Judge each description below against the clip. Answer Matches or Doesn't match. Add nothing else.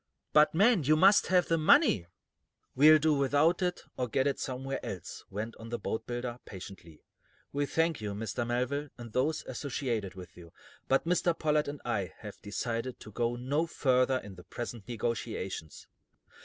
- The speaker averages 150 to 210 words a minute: Matches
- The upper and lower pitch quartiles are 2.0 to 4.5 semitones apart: Doesn't match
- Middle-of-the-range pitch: Doesn't match